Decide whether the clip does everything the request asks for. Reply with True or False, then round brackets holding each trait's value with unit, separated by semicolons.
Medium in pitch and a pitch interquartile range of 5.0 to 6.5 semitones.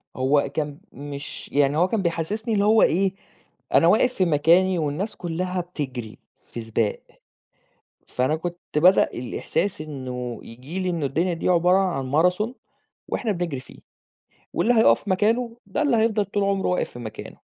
True (175 Hz; 5.6 semitones)